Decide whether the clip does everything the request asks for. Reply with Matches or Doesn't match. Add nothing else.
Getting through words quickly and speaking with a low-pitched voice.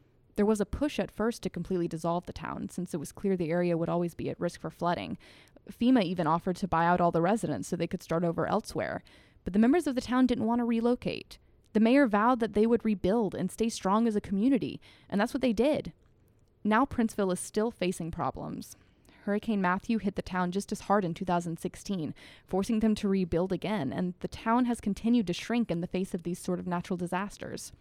Doesn't match